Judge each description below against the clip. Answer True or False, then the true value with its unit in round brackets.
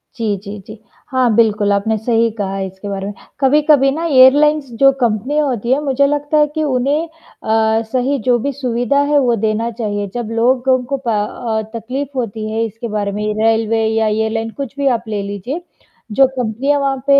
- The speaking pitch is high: True (235 Hz)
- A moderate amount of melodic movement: True (4.0 semitones)